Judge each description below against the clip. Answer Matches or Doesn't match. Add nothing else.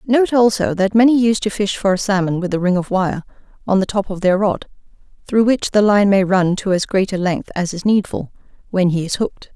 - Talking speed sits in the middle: Doesn't match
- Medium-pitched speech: Doesn't match